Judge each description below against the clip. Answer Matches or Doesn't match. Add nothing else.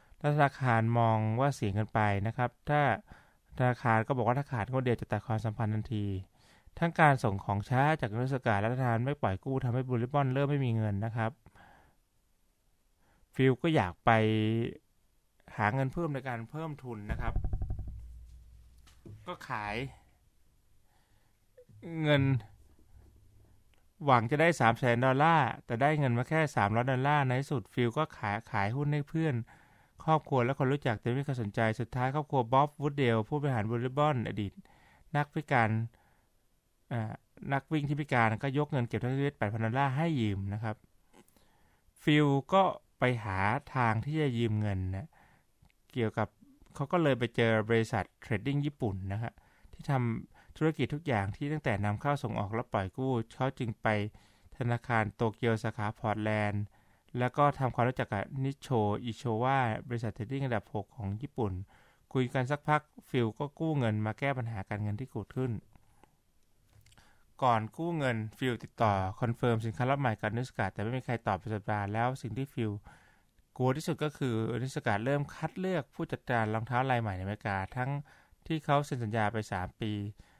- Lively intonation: Doesn't match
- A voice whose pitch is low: Matches